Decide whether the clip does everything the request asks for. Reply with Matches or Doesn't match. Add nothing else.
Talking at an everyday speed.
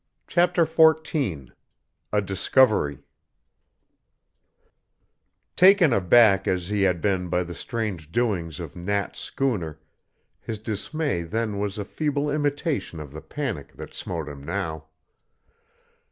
Doesn't match